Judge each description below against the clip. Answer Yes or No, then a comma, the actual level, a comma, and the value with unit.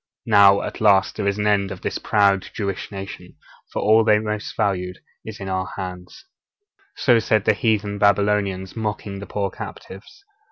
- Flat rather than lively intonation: Yes, narrow, 1.6 semitones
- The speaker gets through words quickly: No, average, 175 wpm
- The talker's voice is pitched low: Yes, low, 100 Hz